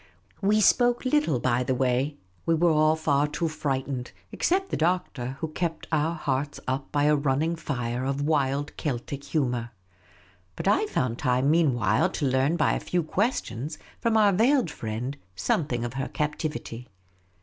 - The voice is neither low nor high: Yes, medium, 145 Hz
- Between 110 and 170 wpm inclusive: Yes, average, 160 wpm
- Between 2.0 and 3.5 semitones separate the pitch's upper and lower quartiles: No, average, 4.3 semitones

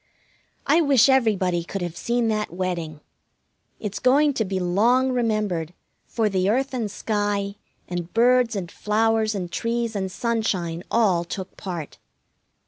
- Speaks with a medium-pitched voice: No, high, 210 Hz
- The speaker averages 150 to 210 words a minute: No, average, 140 wpm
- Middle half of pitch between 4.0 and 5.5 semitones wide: Yes, average, 4.4 semitones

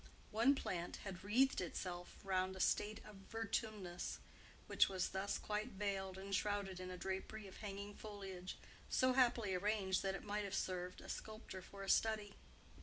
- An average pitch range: No, narrow, 2.1 semitones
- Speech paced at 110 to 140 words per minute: No, average, 170 wpm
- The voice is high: Yes, high, 195 Hz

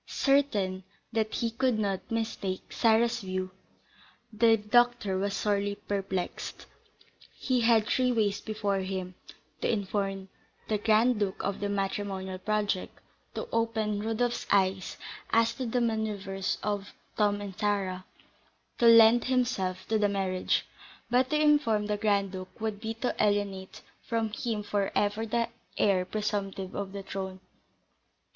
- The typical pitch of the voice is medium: No, high, 210 Hz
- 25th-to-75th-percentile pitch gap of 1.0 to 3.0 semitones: Yes, narrow, 2.6 semitones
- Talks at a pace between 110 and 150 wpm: Yes, average, 140 wpm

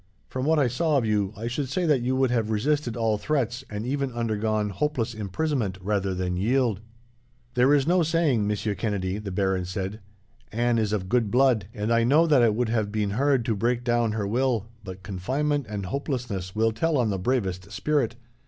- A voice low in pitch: Yes, low, 115 Hz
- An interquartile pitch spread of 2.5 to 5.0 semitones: Yes, average, 4.2 semitones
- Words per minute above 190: Yes, average, 200 wpm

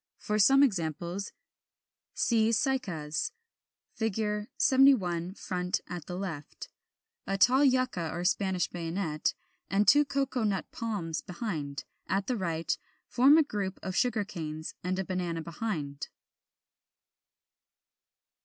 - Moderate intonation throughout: Yes, average, 5.0 semitones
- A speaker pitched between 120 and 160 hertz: No, high, 190 Hz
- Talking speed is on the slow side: Yes, slow, 115 wpm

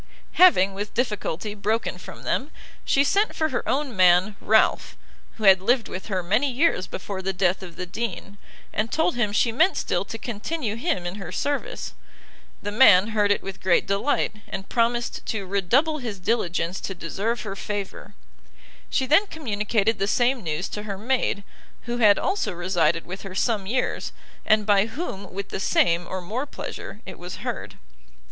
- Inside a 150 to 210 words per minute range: Yes, average, 180 wpm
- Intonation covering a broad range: No, average, 4.2 semitones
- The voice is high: Yes, high, 210 Hz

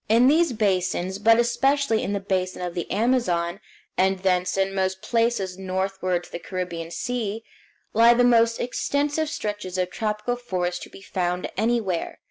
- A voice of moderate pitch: No, high, 195 Hz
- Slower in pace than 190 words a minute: Yes, average, 160 wpm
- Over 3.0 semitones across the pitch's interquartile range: Yes, average, 4.3 semitones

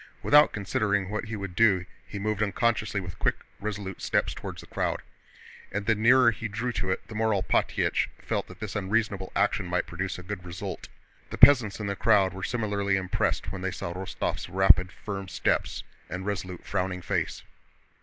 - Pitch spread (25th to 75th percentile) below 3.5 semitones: Yes, narrow, 2.4 semitones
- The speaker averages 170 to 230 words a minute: Yes, average, 180 wpm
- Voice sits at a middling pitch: No, low, 100 Hz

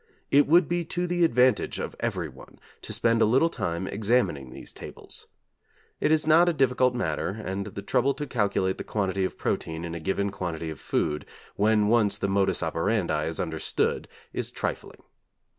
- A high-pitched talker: No, low, 105 Hz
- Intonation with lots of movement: Yes, wide, 6.3 semitones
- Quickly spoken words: No, average, 175 wpm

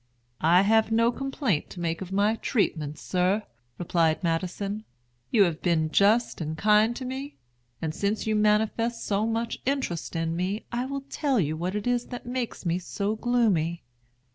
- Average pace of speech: Yes, average, 170 wpm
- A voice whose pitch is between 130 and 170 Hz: No, high, 210 Hz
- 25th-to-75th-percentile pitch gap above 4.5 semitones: Yes, average, 5.3 semitones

